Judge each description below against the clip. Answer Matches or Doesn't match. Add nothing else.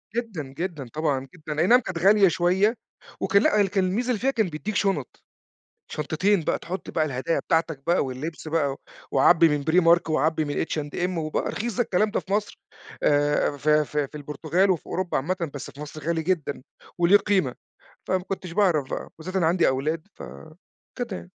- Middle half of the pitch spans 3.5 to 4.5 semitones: Matches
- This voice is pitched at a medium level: Matches